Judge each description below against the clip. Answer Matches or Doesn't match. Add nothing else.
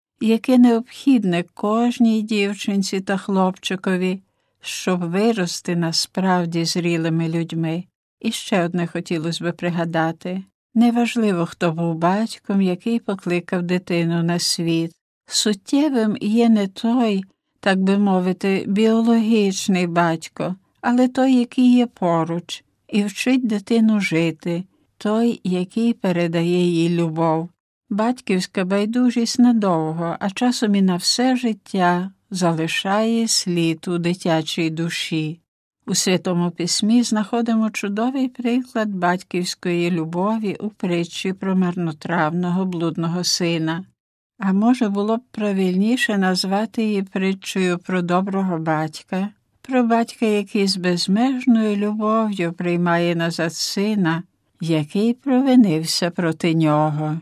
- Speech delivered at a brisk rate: Doesn't match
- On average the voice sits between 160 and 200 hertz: Matches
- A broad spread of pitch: Doesn't match